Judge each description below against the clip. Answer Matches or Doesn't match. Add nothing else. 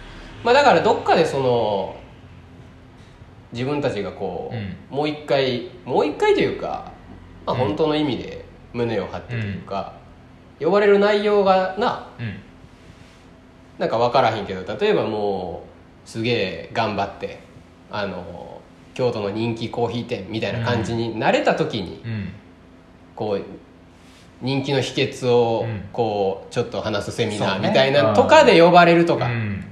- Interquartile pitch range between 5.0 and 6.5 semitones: Matches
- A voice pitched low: Matches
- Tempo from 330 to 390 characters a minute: Doesn't match